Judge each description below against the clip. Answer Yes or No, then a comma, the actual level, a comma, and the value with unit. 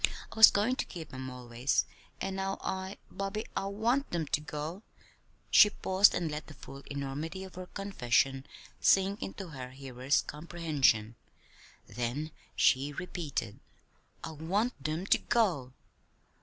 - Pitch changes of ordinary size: No, wide, 6.1 semitones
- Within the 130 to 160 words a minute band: Yes, average, 140 wpm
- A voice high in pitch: No, medium, 160 Hz